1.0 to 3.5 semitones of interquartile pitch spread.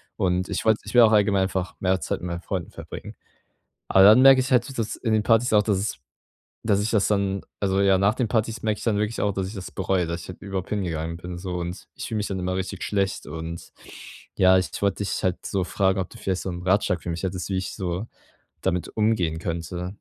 Yes: average, 2.7 semitones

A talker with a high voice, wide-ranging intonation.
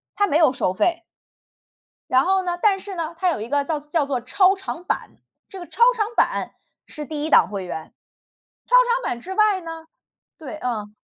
Yes: very high, 325 Hz; wide, 5.8 semitones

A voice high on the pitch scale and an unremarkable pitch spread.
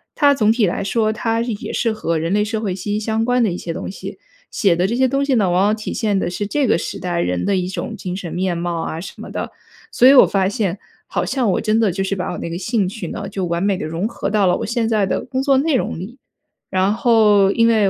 Yes: high, 205 Hz; average, 3.7 semitones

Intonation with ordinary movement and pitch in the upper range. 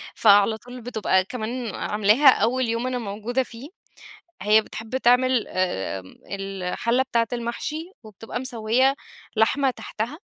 Yes: average, 3.1 semitones; high, 230 Hz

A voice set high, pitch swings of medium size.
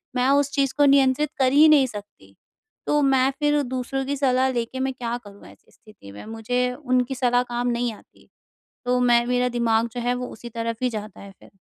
No: very high, 250 Hz; narrow, 2.3 semitones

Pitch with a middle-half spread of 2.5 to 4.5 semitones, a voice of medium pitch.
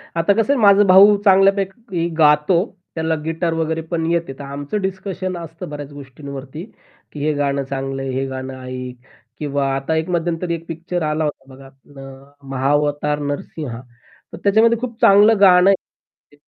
No: average, 4.9 semitones; medium, 160 Hz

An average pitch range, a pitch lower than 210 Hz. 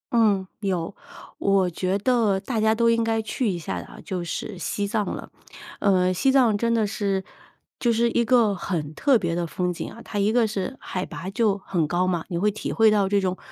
Yes: average, 3.4 semitones; high, 200 Hz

